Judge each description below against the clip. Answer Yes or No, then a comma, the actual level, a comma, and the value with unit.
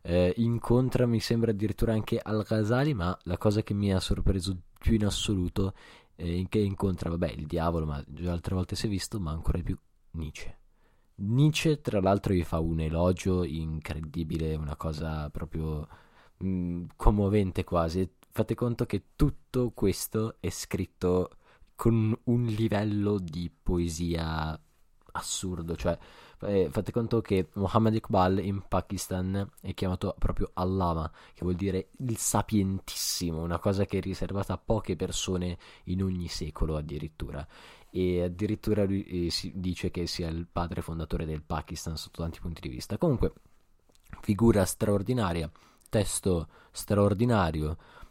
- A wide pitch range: No, average, 3.7 semitones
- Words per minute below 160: Yes, average, 145 wpm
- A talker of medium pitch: No, very low, 95 Hz